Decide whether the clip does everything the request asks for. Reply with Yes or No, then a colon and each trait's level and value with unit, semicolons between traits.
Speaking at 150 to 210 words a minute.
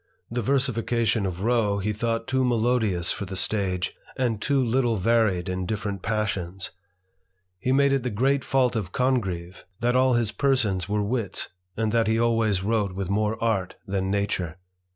Yes: average, 180 wpm